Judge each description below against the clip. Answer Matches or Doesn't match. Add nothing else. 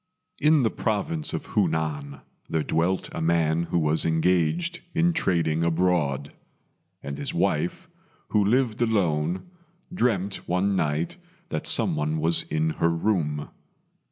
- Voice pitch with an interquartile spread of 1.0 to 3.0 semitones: Doesn't match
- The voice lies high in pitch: Doesn't match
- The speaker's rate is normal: Doesn't match